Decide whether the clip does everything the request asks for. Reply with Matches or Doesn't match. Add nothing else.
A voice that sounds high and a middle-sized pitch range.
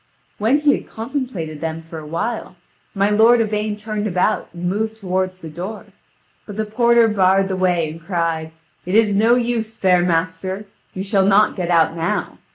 Matches